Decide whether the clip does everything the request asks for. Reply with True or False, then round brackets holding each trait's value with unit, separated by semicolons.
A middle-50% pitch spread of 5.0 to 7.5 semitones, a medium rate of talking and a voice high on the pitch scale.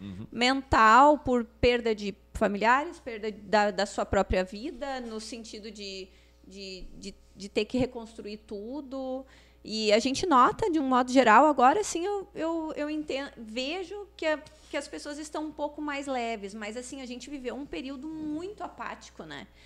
True (5.5 semitones; 170 wpm; 255 Hz)